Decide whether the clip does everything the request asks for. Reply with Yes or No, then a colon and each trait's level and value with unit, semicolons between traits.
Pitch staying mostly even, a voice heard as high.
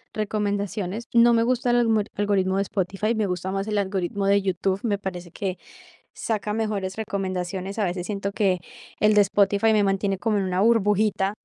Yes: narrow, 2.0 semitones; high, 200 Hz